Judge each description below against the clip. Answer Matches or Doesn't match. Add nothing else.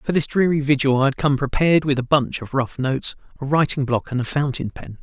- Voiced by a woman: Doesn't match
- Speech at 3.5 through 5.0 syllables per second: Doesn't match